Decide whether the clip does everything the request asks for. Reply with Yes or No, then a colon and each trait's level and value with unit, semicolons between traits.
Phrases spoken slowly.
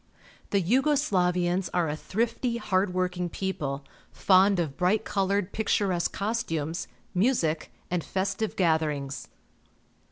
Yes: slow, 115 wpm